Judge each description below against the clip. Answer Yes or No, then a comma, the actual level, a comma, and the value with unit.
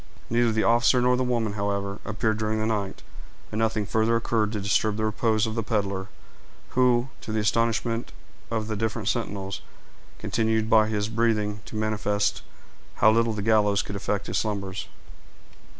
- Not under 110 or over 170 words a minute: Yes, average, 165 wpm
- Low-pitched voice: Yes, low, 110 Hz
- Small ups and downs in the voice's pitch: Yes, narrow, 1.7 semitones